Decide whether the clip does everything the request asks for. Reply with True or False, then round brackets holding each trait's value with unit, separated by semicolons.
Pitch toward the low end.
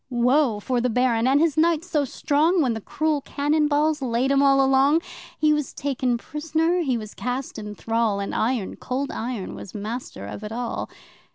False (265 Hz)